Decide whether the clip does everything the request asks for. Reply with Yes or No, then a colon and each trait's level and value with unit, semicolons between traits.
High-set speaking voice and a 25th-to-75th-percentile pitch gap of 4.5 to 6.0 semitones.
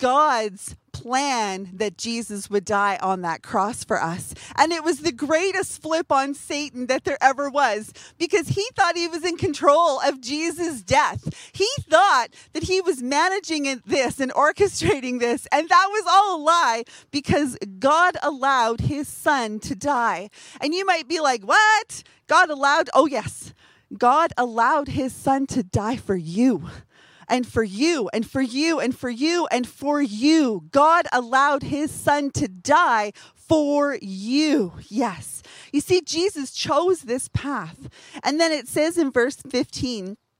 Yes: very high, 280 Hz; average, 5.1 semitones